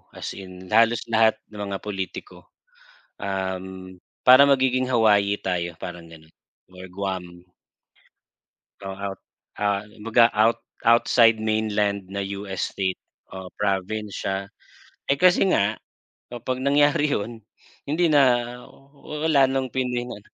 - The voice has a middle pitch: No, low, 105 Hz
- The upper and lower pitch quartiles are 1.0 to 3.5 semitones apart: No, average, 4.3 semitones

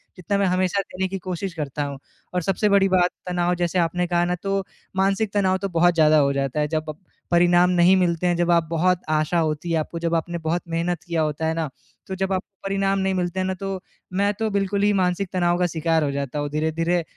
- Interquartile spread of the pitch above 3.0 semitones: No, narrow, 2.5 semitones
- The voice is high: No, medium, 175 Hz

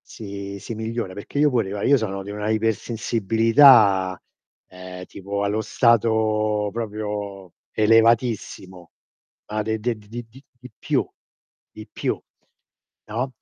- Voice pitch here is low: Yes, low, 110 Hz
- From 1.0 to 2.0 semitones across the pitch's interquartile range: No, narrow, 2.4 semitones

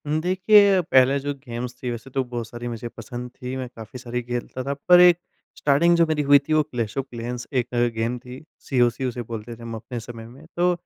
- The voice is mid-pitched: No, low, 125 Hz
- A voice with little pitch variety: No, average, 3.3 semitones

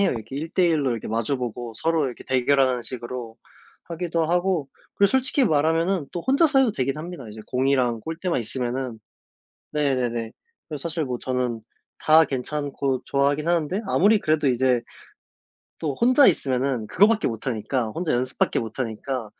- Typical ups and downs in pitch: Yes, average, 5.0 semitones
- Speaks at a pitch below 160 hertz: Yes, medium, 140 Hz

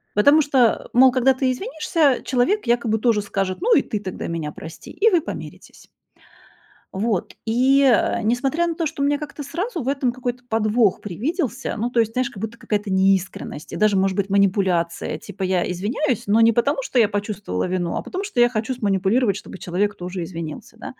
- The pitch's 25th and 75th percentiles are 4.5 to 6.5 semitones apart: Yes, wide, 5.4 semitones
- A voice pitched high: Yes, high, 230 Hz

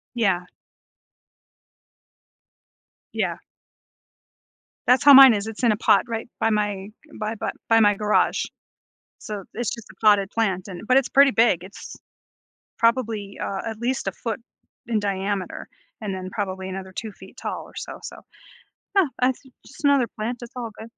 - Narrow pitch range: No, average, 3.1 semitones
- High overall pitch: Yes, high, 215 Hz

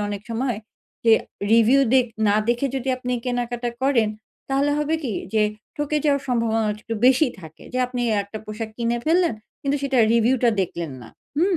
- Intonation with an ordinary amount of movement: Yes, average, 3.4 semitones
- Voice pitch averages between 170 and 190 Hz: No, high, 245 Hz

